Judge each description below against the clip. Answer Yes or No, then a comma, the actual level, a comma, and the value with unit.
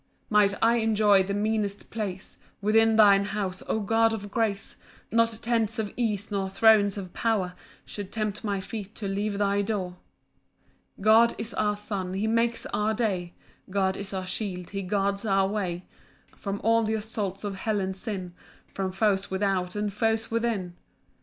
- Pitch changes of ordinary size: No, narrow, 2.2 semitones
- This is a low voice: No, high, 205 Hz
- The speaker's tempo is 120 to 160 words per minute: No, average, 170 wpm